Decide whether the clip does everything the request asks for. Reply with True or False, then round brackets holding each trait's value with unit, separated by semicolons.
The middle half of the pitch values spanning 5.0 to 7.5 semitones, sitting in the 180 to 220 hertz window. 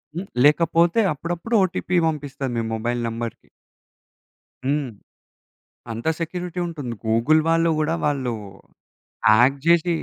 False (5.3 semitones; 150 Hz)